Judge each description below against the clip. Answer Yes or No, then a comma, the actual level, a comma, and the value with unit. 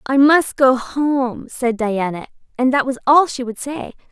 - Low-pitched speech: No, very high, 260 Hz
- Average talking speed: Yes, average, 190 wpm